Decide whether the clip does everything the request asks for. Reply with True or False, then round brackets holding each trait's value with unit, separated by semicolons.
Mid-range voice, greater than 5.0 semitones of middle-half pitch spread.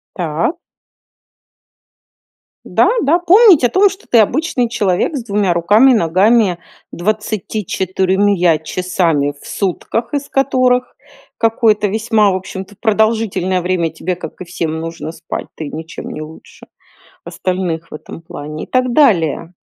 False (195 Hz; 5.4 semitones)